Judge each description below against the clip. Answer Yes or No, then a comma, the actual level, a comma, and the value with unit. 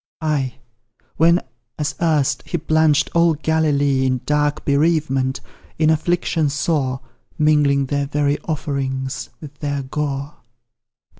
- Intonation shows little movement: Yes, narrow, 2.1 semitones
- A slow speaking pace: Yes, slow, 115 wpm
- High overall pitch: No, medium, 145 Hz